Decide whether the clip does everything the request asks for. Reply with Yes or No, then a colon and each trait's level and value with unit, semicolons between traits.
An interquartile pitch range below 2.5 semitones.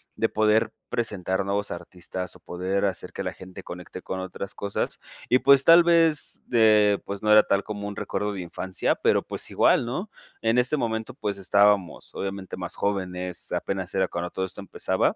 No: average, 2.9 semitones